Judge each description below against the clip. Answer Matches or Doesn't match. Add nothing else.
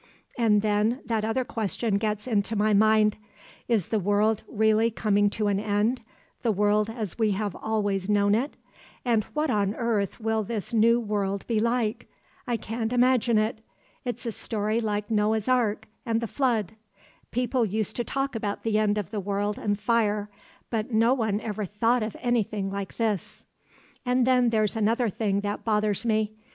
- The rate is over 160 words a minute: Matches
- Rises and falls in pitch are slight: Matches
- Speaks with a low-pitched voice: Doesn't match